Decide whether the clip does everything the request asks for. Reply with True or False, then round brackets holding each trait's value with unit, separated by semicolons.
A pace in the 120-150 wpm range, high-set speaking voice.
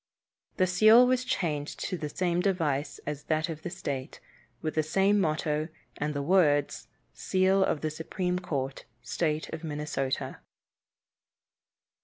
False (140 wpm; 160 Hz)